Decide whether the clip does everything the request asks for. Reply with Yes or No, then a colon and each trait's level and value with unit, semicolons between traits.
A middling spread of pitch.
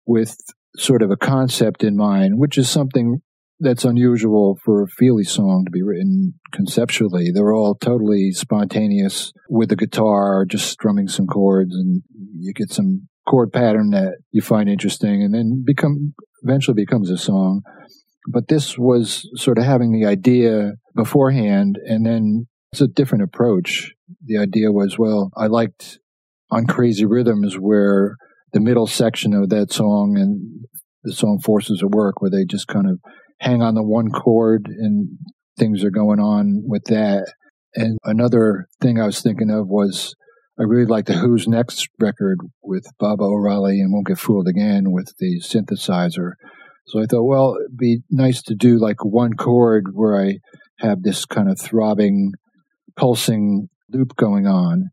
No: wide, 6.5 semitones